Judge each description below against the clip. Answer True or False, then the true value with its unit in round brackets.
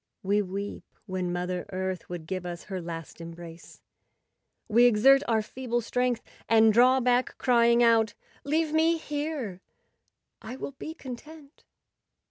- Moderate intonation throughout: False (5.8 semitones)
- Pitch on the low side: False (230 Hz)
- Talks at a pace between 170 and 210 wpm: False (140 wpm)